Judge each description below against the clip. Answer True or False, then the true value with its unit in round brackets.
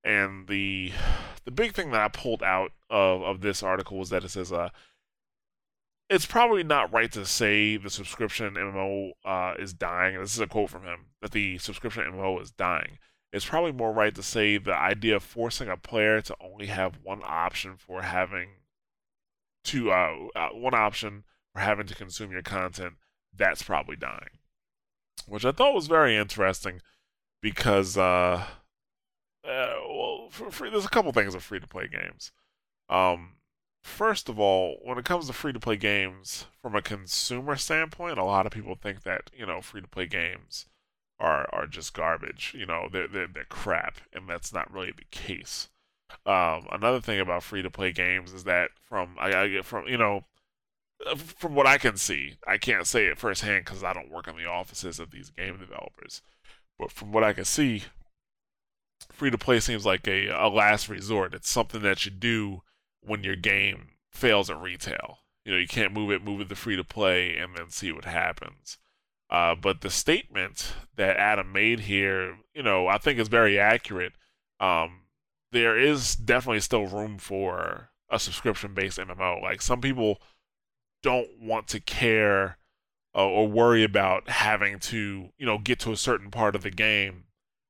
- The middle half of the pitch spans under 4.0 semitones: True (3.4 semitones)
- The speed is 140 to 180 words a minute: True (175 wpm)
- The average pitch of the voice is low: True (100 Hz)